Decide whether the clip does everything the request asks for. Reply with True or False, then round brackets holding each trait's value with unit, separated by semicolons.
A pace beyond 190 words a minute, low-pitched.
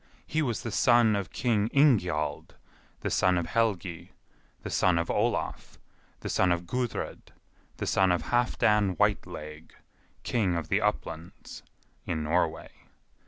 False (135 wpm; 95 Hz)